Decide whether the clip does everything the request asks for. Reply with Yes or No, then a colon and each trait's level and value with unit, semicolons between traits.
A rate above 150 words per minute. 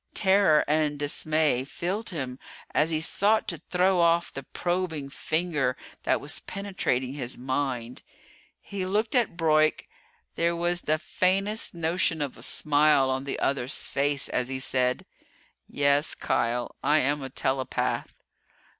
No: average, 140 wpm